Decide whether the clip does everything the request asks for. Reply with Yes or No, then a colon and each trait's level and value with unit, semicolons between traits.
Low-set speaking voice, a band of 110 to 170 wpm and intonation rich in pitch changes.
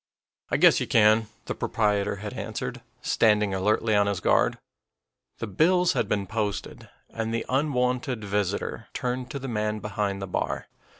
No: low, 110 Hz; average, 160 wpm; average, 3.3 semitones